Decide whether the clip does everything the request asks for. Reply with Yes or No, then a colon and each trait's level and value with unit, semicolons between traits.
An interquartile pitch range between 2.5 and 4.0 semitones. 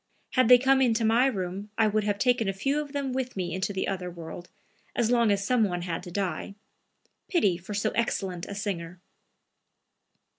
No: average, 5.0 semitones